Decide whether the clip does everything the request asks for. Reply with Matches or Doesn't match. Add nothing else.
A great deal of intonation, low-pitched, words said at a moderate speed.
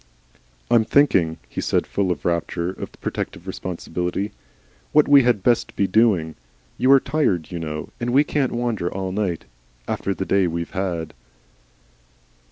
Matches